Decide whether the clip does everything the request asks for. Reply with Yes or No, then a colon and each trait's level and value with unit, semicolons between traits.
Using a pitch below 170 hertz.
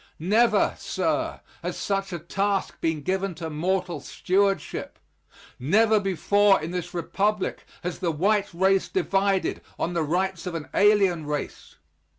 No: high, 190 Hz